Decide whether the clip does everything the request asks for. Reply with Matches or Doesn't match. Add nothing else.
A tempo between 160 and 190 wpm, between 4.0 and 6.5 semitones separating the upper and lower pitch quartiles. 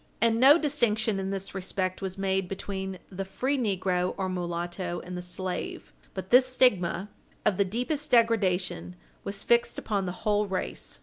Doesn't match